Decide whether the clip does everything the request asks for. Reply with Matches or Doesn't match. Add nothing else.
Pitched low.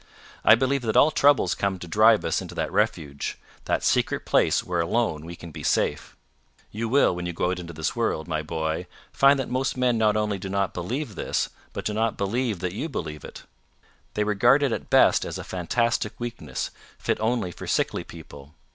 Matches